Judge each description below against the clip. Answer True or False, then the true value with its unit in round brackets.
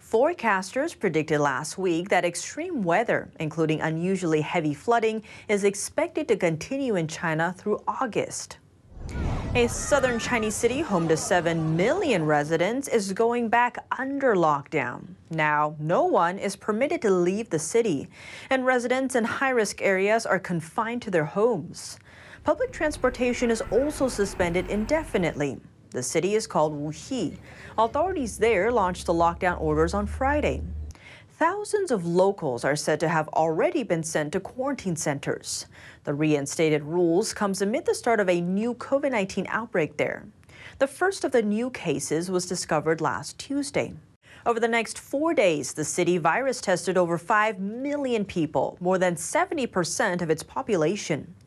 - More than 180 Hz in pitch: True (190 Hz)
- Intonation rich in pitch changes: True (7.1 semitones)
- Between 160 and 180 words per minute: False (150 wpm)